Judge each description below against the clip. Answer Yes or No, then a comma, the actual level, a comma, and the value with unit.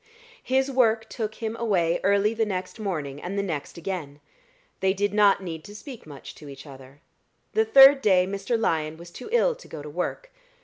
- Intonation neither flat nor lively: No, wide, 5.9 semitones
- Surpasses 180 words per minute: Yes, average, 195 wpm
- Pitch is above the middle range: Yes, high, 195 Hz